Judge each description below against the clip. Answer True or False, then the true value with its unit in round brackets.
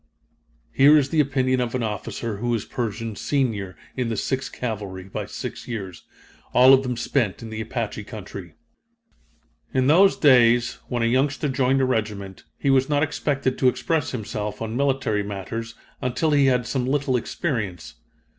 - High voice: False (125 Hz)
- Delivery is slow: False (165 wpm)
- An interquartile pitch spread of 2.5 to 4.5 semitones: True (3.8 semitones)